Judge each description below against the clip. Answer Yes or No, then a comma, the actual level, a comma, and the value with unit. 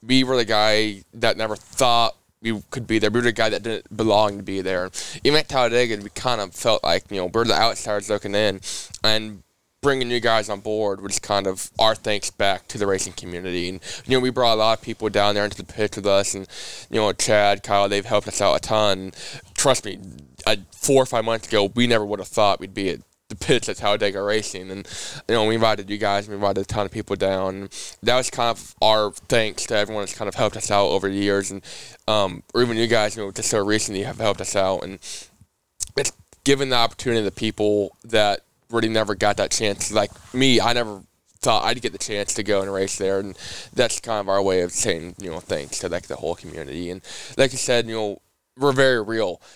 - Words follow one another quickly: Yes, fast, 245 wpm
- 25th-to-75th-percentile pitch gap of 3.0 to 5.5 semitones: No, narrow, 2.5 semitones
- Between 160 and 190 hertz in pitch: No, low, 105 Hz